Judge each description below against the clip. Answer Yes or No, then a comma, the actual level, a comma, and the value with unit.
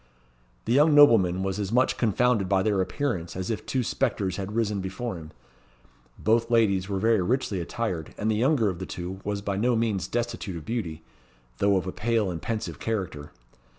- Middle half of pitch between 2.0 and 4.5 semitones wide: Yes, average, 3.7 semitones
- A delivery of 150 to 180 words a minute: No, average, 190 wpm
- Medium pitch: No, low, 105 Hz